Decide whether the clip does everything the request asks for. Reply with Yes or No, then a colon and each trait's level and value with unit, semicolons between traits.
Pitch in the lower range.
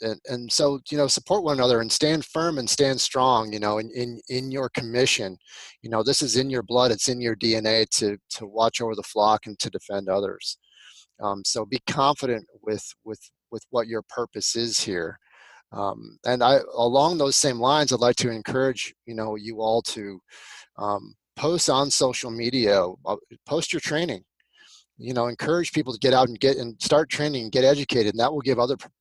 Yes: low, 125 Hz